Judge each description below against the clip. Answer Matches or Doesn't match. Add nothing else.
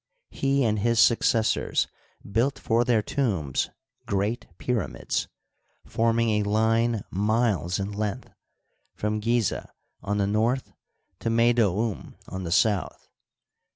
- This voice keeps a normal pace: Doesn't match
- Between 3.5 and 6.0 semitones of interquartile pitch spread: Doesn't match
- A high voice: Doesn't match